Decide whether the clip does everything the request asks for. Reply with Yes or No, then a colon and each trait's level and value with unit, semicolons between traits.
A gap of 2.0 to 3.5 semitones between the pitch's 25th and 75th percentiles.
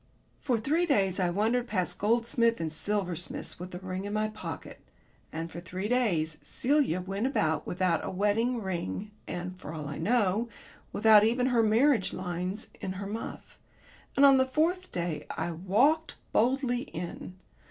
No: average, 5.2 semitones